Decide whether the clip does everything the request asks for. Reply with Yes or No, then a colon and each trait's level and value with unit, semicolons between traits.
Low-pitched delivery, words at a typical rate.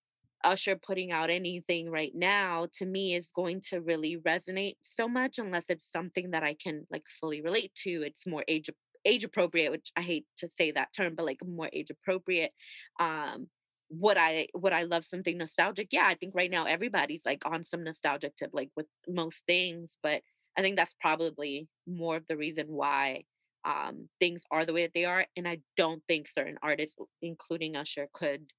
No: medium, 170 Hz; average, 195 wpm